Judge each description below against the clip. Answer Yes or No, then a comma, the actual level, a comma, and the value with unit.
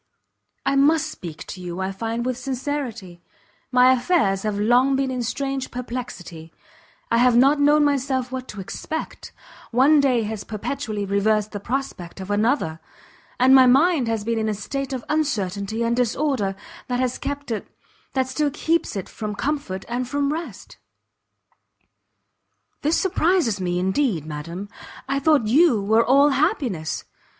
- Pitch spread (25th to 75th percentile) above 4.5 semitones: Yes, average, 5.2 semitones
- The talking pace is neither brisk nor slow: Yes, average, 155 wpm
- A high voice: Yes, high, 245 Hz